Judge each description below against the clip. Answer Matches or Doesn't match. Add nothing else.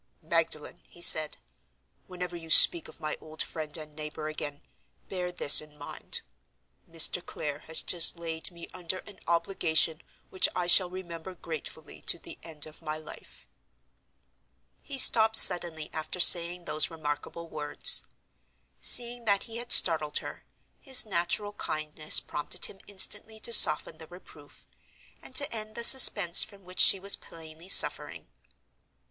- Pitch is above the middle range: Doesn't match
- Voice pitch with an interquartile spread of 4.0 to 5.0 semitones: Doesn't match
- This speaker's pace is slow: Doesn't match